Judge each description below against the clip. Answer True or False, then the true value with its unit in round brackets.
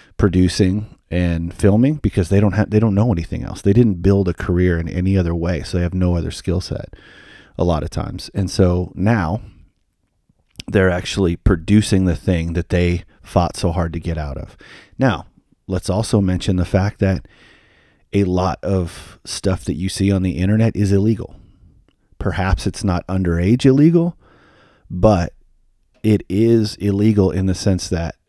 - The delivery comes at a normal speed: True (170 wpm)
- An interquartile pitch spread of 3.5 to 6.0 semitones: False (2.7 semitones)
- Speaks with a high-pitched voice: False (95 Hz)